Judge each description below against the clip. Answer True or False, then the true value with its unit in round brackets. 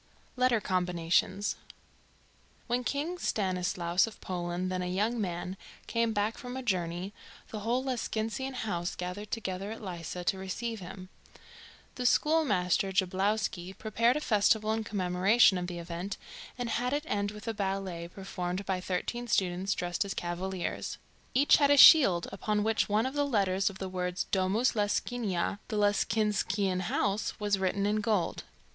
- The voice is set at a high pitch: True (200 Hz)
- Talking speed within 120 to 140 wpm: False (155 wpm)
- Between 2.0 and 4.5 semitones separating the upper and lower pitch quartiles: True (3.5 semitones)